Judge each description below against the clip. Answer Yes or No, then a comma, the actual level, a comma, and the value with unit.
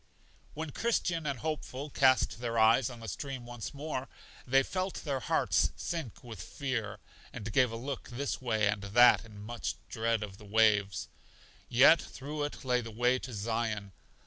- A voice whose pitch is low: Yes, low, 120 Hz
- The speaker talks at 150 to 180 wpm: Yes, average, 170 wpm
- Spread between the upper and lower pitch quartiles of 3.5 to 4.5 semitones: Yes, average, 3.8 semitones